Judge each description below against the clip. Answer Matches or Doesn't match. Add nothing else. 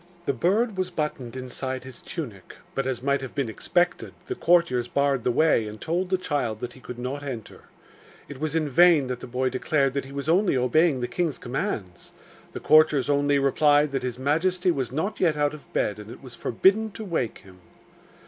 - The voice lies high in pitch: Doesn't match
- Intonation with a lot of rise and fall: Doesn't match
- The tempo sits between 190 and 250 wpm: Matches